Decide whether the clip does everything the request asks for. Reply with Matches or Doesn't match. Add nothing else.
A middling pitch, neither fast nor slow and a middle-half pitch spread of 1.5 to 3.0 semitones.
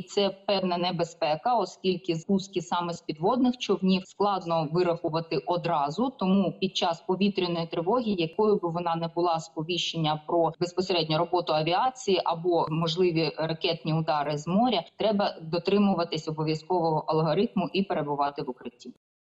Matches